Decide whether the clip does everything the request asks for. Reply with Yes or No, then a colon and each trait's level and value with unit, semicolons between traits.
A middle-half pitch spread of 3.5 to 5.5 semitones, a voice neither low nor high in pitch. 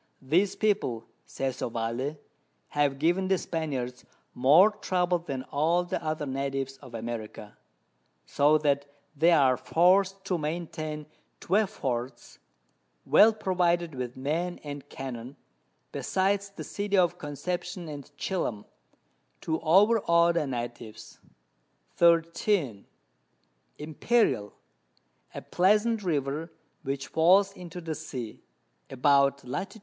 Yes: average, 5.0 semitones; medium, 155 Hz